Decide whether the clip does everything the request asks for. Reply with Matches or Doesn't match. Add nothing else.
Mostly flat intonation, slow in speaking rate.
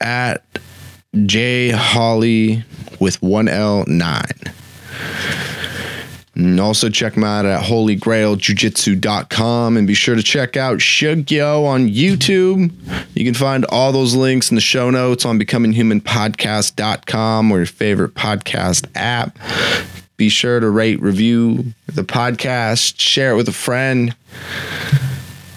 Doesn't match